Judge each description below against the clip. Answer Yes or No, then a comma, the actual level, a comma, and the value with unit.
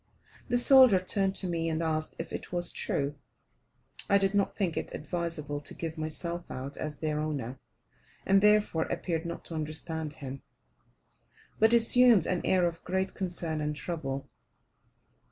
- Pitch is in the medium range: Yes, medium, 170 Hz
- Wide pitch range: No, average, 3.7 semitones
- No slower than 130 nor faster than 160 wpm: Yes, average, 155 wpm